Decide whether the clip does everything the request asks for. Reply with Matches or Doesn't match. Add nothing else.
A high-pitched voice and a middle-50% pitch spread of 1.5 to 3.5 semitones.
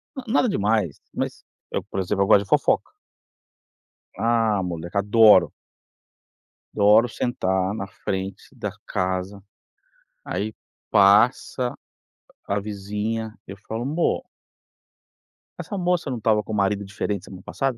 Doesn't match